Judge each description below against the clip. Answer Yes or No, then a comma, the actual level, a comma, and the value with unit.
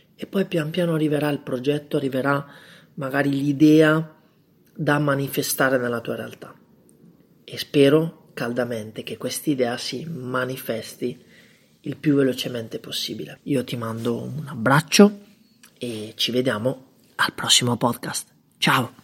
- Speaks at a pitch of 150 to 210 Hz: No, medium, 140 Hz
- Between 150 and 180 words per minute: No, average, 125 wpm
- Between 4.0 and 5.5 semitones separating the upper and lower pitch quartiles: No, average, 3.5 semitones